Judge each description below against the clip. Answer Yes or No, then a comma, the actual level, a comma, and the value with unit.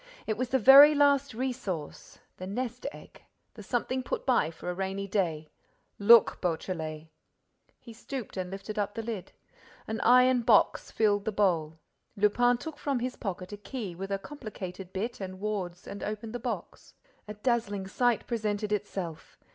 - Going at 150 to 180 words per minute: Yes, average, 165 wpm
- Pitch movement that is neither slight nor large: Yes, average, 4.3 semitones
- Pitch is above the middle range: Yes, high, 210 Hz